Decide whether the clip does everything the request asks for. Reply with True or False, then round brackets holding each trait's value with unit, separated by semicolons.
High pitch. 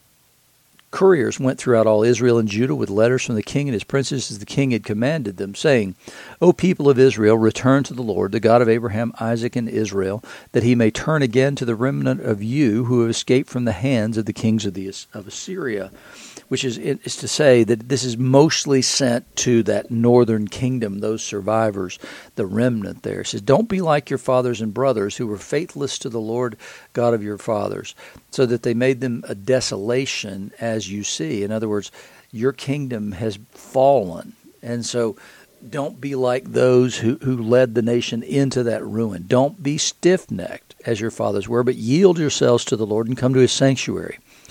False (120 Hz)